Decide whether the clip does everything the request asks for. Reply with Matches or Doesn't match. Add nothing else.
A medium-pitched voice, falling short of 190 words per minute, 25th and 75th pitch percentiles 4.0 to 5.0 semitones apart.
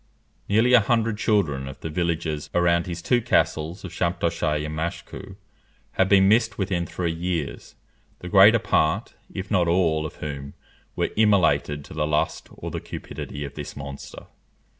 Doesn't match